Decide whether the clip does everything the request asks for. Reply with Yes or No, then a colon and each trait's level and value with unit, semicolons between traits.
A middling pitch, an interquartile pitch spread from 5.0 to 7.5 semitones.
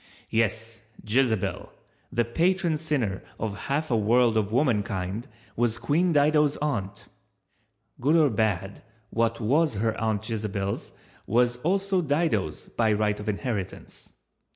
No: low, 115 Hz; wide, 5.5 semitones